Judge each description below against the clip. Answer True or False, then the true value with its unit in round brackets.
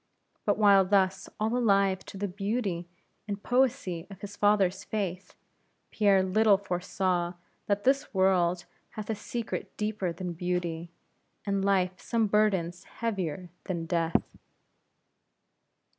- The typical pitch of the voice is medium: False (195 Hz)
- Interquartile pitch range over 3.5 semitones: False (2.8 semitones)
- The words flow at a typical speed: False (125 wpm)